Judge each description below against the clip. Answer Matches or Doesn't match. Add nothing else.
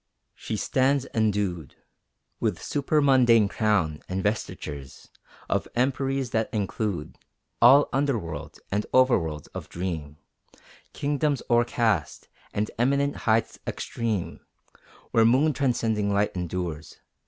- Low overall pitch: Matches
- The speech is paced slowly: Matches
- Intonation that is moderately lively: Doesn't match